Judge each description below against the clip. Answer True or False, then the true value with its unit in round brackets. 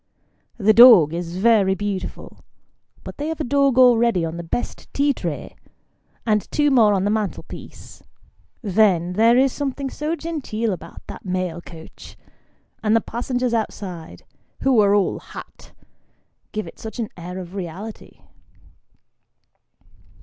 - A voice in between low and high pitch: False (215 Hz)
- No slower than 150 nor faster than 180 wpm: False (140 wpm)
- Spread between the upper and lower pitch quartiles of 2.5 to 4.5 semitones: False (5.2 semitones)